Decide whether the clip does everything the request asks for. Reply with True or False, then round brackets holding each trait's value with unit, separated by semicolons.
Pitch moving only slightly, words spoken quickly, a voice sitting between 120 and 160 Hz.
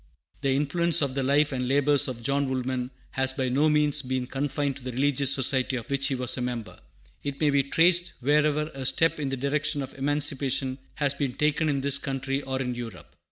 True (1.9 semitones; 210 wpm; 140 Hz)